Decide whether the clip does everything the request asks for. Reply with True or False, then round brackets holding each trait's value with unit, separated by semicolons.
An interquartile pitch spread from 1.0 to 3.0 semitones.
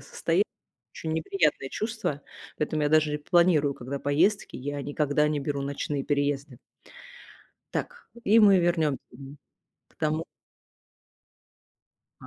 True (2.5 semitones)